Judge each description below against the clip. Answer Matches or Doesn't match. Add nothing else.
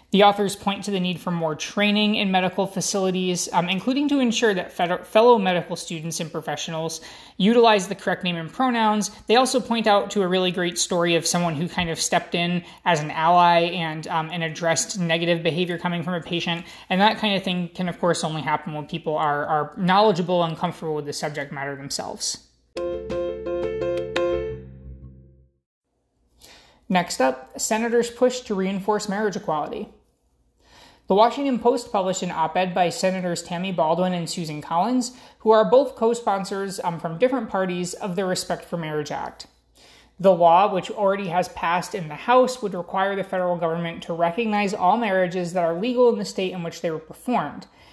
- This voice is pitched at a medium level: Matches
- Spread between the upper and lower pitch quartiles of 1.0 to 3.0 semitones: Doesn't match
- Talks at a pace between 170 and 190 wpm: Matches